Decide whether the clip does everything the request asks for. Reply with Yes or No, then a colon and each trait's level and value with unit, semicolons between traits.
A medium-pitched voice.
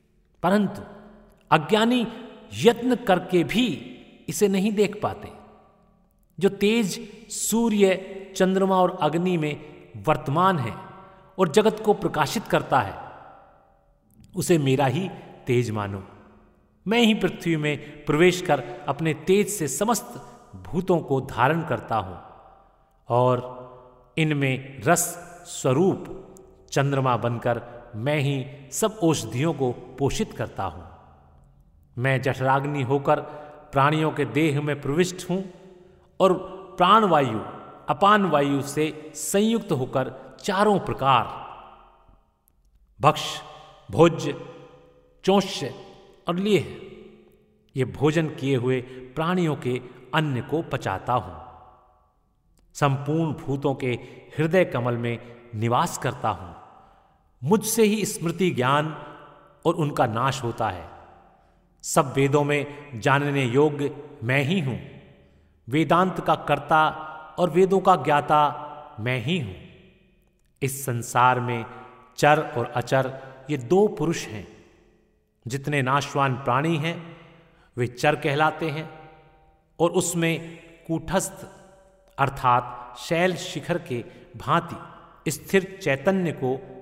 Yes: medium, 150 Hz